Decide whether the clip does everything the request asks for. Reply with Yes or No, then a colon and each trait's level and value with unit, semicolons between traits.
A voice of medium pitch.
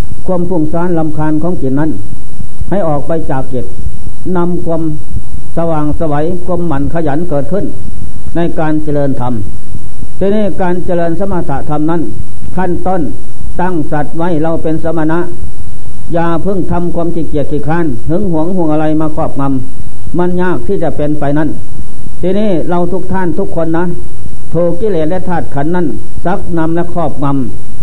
Yes: medium, 160 Hz